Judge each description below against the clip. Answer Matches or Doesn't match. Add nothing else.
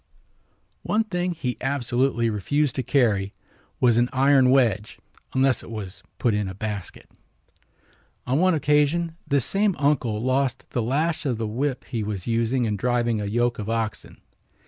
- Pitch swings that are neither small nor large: Matches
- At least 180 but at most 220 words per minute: Doesn't match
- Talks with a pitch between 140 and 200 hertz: Doesn't match